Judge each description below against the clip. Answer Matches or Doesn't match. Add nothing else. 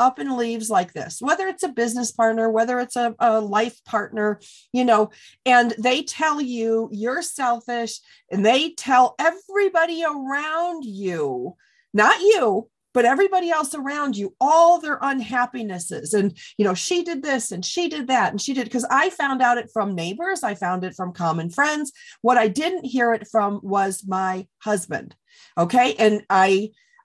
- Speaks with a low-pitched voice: Doesn't match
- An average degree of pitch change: Doesn't match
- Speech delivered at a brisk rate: Doesn't match